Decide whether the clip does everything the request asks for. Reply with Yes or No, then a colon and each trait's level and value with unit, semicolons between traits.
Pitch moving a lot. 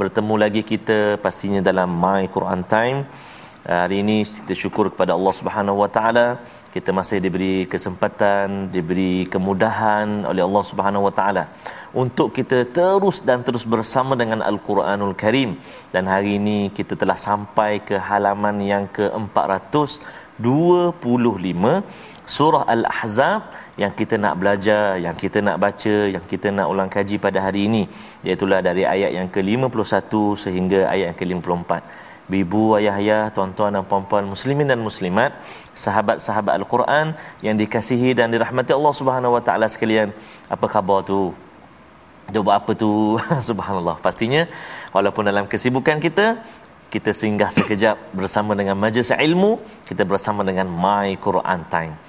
No: average, 2.8 semitones